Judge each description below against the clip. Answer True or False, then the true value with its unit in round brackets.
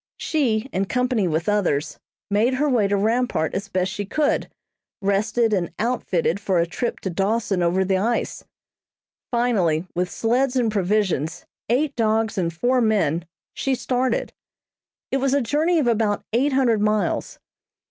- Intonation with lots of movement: False (4.6 semitones)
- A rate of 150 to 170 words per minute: True (155 wpm)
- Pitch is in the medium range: False (215 Hz)